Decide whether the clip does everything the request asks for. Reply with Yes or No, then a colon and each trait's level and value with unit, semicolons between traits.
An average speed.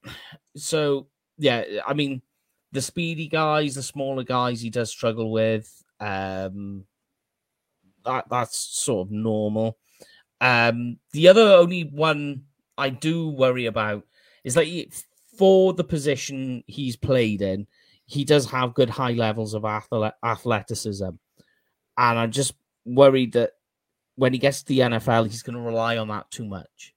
Yes: average, 145 wpm